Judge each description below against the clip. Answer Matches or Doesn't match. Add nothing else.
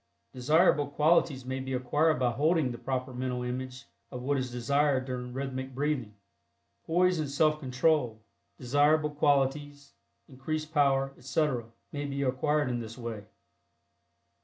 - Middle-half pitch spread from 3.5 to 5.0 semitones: Doesn't match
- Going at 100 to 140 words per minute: Matches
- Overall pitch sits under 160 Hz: Matches